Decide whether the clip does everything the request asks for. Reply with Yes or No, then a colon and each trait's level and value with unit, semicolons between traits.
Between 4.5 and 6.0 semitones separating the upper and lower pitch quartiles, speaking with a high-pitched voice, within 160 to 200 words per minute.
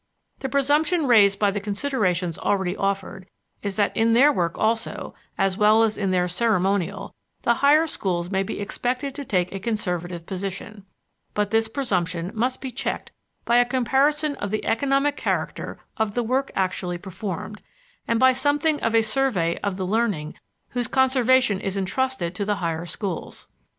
Yes: wide, 5.5 semitones; high, 210 Hz; average, 165 wpm